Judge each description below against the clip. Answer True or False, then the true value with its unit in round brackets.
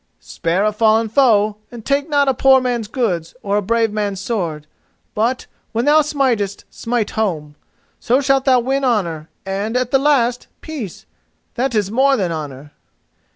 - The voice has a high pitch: True (225 Hz)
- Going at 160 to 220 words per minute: True (165 wpm)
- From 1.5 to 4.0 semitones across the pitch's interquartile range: False (4.7 semitones)